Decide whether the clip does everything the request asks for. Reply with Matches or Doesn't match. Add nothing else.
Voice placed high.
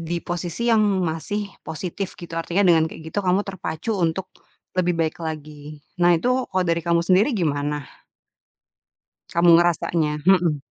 Doesn't match